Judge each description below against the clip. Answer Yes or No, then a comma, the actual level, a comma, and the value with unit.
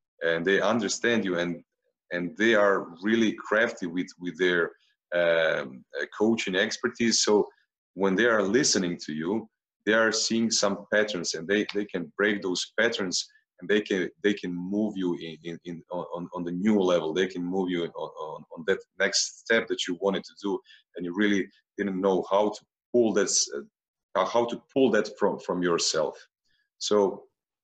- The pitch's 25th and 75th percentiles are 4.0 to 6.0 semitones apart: Yes, average, 4.4 semitones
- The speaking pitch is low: Yes, low, 100 Hz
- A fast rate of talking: Yes, fast, 180 wpm